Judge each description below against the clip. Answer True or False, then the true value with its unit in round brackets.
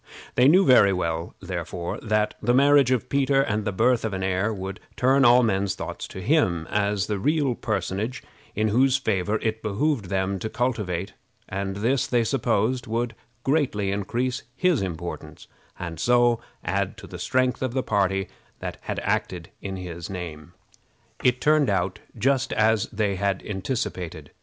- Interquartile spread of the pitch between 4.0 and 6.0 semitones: True (4.8 semitones)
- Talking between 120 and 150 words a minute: False (160 wpm)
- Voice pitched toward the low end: True (110 Hz)